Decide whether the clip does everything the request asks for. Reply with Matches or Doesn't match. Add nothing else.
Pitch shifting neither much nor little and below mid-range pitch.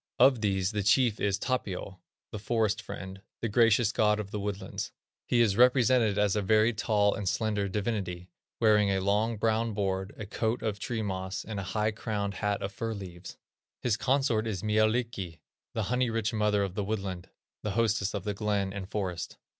Doesn't match